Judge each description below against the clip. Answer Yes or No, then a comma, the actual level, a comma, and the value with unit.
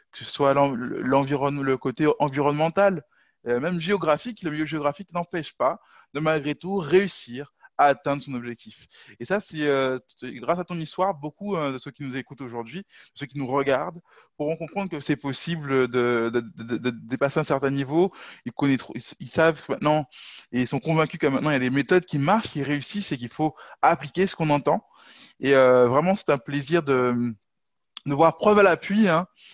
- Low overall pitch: No, medium, 145 Hz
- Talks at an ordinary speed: Yes, average, 195 wpm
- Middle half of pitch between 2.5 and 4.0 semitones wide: Yes, average, 3.7 semitones